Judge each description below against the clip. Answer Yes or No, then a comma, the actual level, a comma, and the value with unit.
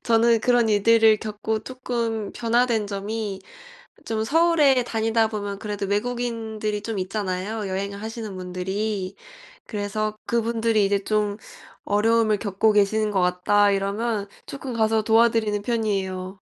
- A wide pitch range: No, narrow, 2.1 semitones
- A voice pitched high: Yes, high, 215 Hz